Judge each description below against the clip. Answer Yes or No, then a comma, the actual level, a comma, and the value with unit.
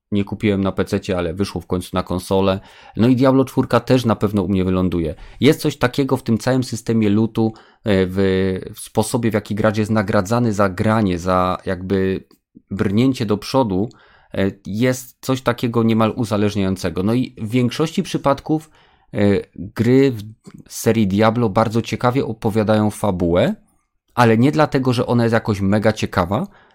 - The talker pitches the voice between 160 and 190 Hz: No, low, 110 Hz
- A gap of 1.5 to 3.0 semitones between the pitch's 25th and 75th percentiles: No, average, 4.2 semitones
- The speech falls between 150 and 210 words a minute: Yes, average, 155 wpm